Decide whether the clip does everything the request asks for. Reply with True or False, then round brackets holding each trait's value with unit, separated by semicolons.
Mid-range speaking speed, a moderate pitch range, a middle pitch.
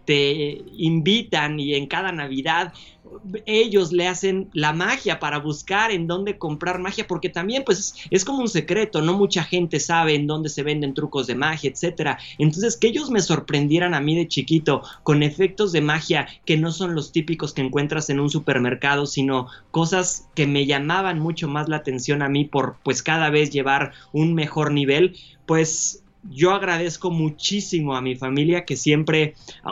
True (175 wpm; 3.7 semitones; 155 Hz)